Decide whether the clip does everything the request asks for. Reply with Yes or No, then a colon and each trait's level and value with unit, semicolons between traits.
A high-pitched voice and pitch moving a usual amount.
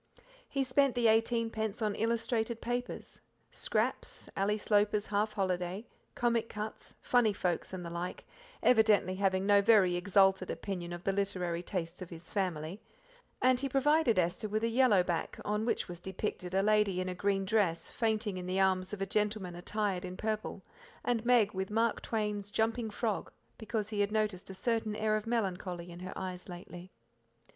Yes: high, 205 Hz; average, 3.2 semitones